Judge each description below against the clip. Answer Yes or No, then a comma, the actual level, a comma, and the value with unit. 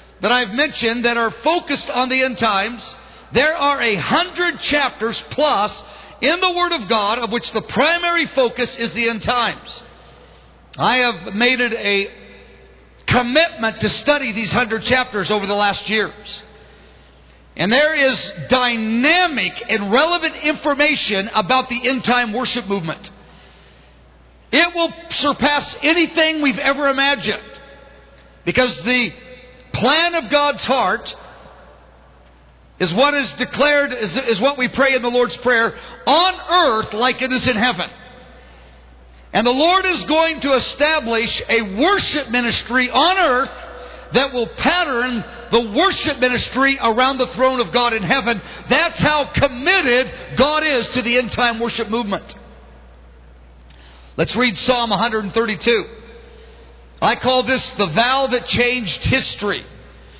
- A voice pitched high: Yes, high, 245 Hz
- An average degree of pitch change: Yes, average, 4.5 semitones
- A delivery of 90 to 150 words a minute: Yes, average, 140 wpm